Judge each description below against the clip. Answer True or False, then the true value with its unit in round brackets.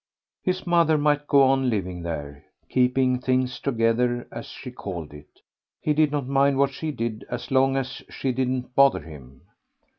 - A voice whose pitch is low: True (130 Hz)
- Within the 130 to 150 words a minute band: False (170 wpm)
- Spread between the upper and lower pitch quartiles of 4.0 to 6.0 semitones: False (3.3 semitones)